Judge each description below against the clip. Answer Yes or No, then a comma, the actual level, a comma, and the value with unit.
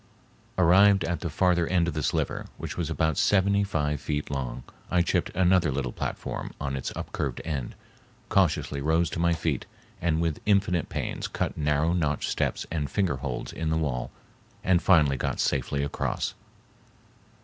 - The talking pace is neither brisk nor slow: Yes, average, 165 wpm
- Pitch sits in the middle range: No, very low, 80 Hz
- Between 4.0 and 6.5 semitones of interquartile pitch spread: No, average, 3.5 semitones